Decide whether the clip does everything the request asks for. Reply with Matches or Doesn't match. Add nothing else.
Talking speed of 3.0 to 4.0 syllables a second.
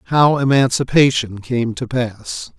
Matches